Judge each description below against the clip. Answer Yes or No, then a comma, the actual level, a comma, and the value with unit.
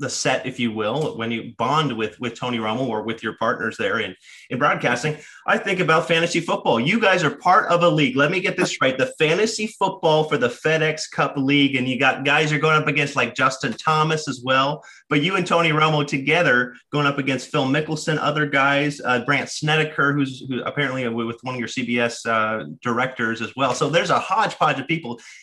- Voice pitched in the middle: Yes, medium, 145 Hz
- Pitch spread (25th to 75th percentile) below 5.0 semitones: Yes, average, 3.9 semitones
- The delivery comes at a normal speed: No, fast, 215 wpm